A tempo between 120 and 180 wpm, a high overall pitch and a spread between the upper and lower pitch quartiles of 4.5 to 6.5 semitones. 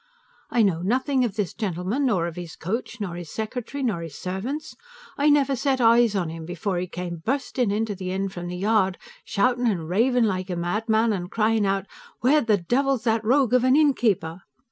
No: average, 200 wpm; high, 215 Hz; wide, 5.4 semitones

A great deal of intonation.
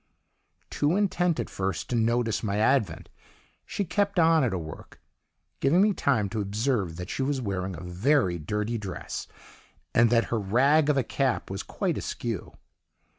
Yes: wide, 6.6 semitones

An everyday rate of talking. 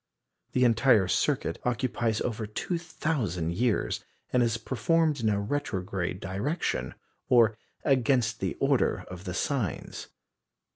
No: slow, 115 wpm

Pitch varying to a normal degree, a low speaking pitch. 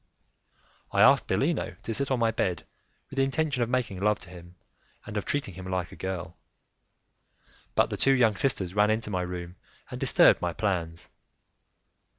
Yes: average, 4.9 semitones; low, 100 Hz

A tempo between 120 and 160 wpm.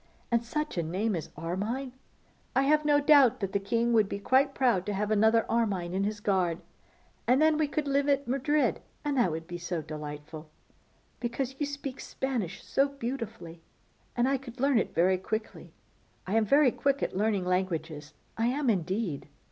No: average, 185 wpm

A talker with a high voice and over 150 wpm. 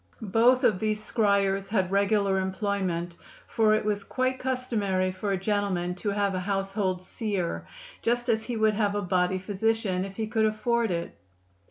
Yes: high, 200 Hz; average, 170 wpm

